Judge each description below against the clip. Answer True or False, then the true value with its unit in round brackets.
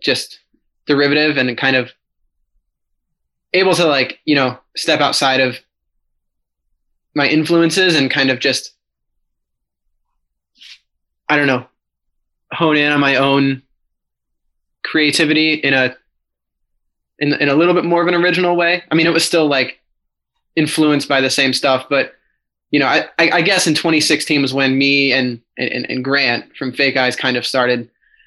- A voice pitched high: False (135 Hz)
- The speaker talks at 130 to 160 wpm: True (155 wpm)